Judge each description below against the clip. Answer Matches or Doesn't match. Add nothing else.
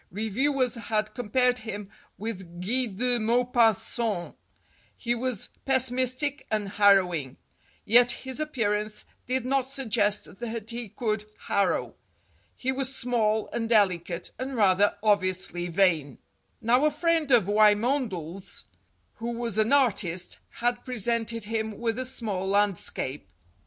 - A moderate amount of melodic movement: Matches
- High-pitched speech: Matches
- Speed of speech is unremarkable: Doesn't match